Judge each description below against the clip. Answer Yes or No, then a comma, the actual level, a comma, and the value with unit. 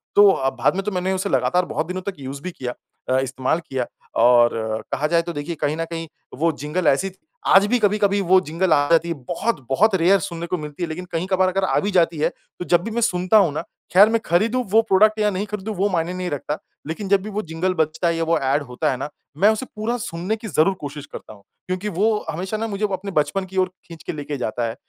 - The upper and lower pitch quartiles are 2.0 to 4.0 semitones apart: No, average, 4.5 semitones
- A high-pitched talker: No, medium, 180 Hz